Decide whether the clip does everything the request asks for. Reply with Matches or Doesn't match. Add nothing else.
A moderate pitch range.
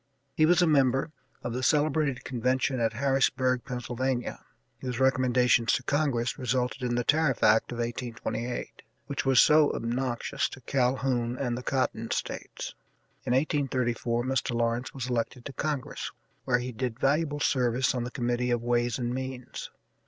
Doesn't match